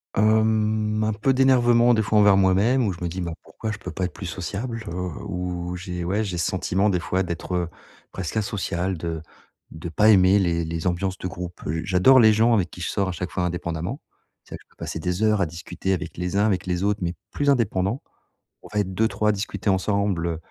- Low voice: Yes, very low, 95 Hz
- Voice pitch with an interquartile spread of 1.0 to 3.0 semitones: No, average, 3.4 semitones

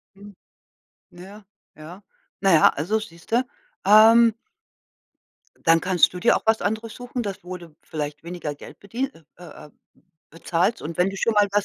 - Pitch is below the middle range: No, high, 195 Hz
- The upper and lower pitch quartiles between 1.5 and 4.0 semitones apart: No, average, 4.4 semitones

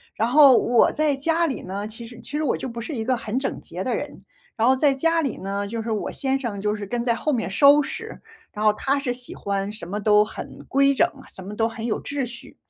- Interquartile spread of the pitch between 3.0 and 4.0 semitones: No, average, 4.6 semitones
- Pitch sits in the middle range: No, high, 235 Hz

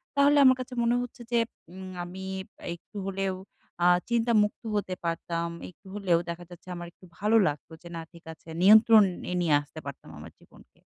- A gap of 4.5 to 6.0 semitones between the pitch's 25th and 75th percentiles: Yes, average, 4.9 semitones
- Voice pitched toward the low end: No, high, 190 Hz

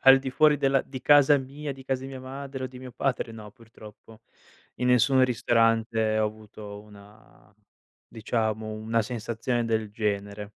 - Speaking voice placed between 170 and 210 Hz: No, low, 115 Hz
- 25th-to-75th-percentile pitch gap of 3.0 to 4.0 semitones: Yes, average, 3.5 semitones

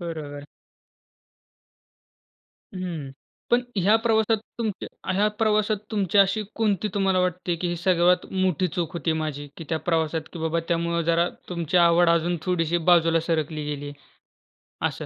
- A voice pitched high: No, medium, 175 Hz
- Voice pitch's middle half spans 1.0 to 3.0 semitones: Yes, narrow, 2.6 semitones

